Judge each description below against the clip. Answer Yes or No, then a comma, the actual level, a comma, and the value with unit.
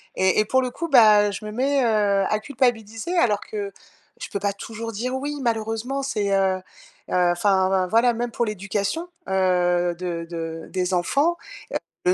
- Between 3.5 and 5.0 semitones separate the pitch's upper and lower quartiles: Yes, average, 4.2 semitones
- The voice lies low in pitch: No, high, 210 Hz